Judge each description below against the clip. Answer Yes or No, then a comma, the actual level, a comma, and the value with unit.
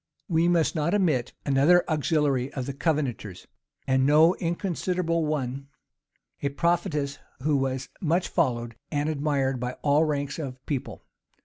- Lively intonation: No, average, 3.5 semitones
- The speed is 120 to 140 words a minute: Yes, slow, 135 wpm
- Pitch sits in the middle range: Yes, medium, 145 Hz